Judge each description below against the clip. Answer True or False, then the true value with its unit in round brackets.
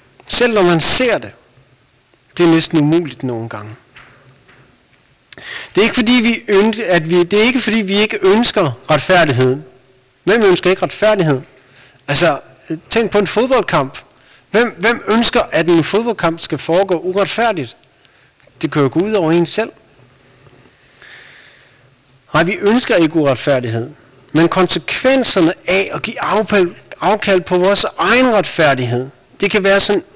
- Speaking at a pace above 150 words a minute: False (145 wpm)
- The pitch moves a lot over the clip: True (7.5 semitones)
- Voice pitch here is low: False (175 Hz)